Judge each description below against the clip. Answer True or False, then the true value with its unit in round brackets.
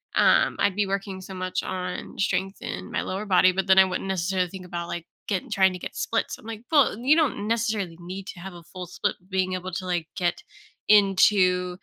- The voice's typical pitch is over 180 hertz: True (190 Hz)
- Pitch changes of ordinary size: False (1.6 semitones)